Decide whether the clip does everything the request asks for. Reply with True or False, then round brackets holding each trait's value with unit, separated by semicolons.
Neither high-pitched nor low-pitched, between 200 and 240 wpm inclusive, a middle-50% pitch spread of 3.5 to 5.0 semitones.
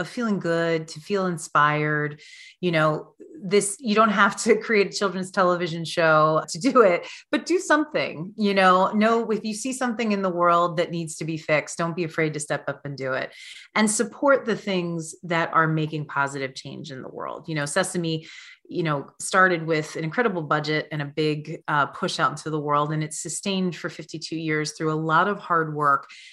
True (170 Hz; 205 wpm; 4.6 semitones)